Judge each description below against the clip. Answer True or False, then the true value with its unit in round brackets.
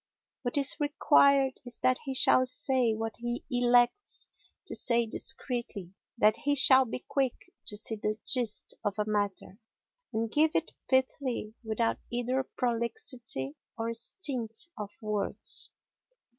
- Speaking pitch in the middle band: False (240 Hz)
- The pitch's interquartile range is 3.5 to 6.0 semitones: False (3.0 semitones)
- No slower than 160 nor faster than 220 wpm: False (135 wpm)